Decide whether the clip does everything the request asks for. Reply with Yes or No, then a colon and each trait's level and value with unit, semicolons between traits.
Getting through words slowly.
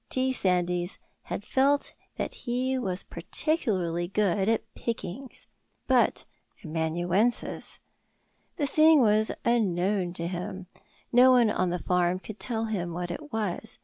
Yes: slow, 130 wpm